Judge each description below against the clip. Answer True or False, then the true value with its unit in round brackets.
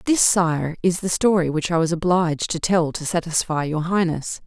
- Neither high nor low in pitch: True (170 Hz)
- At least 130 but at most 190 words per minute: False (200 wpm)